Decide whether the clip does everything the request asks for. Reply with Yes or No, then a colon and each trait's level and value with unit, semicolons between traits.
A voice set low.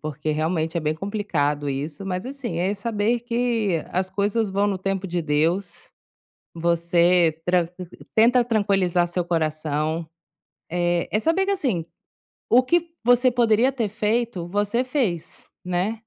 No: high, 190 Hz